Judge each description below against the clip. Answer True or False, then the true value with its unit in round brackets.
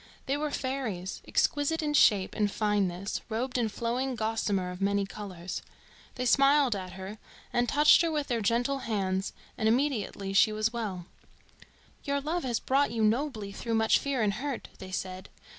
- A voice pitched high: True (225 Hz)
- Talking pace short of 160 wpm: False (170 wpm)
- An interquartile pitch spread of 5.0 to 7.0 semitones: True (5.4 semitones)